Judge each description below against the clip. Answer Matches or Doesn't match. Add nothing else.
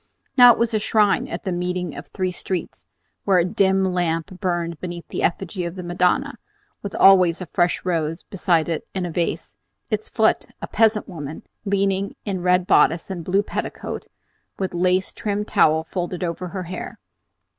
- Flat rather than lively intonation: Matches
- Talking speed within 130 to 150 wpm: Doesn't match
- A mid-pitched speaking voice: Matches